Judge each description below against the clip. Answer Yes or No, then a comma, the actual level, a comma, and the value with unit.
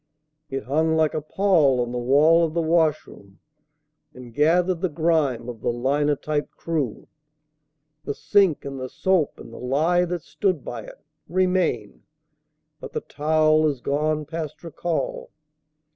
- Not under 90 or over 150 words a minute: Yes, average, 145 wpm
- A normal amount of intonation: Yes, average, 3.6 semitones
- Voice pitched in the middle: Yes, medium, 155 Hz